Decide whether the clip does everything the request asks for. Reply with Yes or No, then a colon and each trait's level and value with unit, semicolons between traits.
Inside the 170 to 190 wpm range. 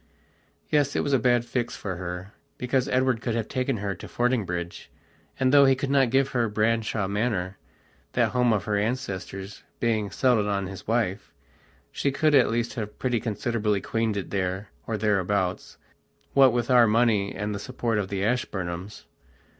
Yes: average, 175 wpm